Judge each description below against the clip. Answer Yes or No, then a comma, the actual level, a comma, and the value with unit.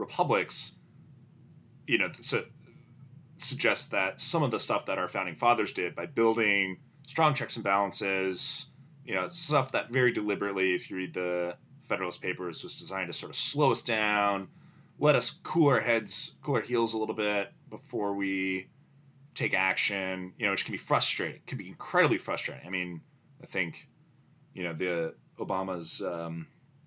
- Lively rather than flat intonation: Yes, wide, 6.5 semitones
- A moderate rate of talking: Yes, average, 165 wpm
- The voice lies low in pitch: Yes, low, 110 Hz